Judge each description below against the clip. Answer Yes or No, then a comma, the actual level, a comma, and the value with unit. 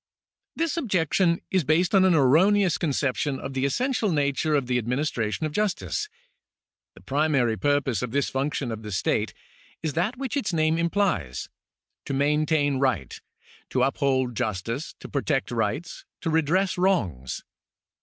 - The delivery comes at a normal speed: Yes, average, 150 wpm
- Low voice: No, medium, 150 Hz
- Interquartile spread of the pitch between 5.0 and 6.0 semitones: Yes, wide, 5.6 semitones